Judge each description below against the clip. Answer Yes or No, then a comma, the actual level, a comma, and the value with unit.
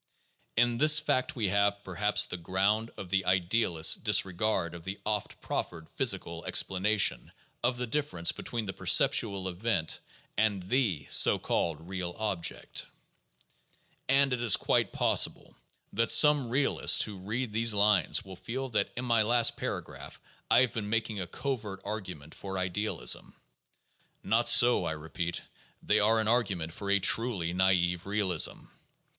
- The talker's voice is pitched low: Yes, low, 100 Hz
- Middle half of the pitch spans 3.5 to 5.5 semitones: Yes, average, 4.0 semitones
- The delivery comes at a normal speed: Yes, average, 150 wpm